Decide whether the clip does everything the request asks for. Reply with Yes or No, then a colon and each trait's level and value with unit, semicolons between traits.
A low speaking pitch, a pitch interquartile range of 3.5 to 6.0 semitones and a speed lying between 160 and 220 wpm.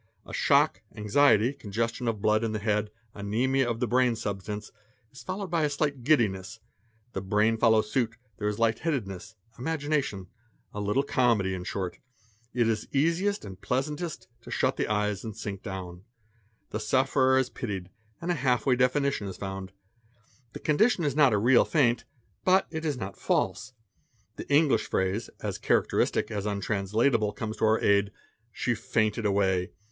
Yes: low, 115 Hz; average, 4.8 semitones; average, 170 wpm